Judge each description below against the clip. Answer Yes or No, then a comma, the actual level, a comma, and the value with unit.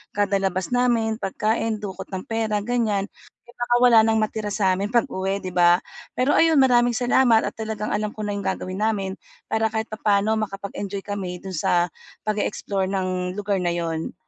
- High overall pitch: Yes, high, 205 Hz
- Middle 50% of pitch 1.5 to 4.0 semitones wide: Yes, narrow, 2.6 semitones